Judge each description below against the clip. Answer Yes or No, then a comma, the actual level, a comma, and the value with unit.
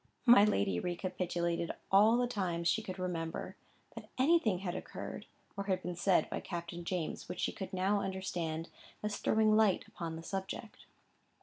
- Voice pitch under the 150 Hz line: No, medium, 185 Hz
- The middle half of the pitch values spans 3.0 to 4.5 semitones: Yes, average, 3.3 semitones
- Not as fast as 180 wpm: Yes, average, 160 wpm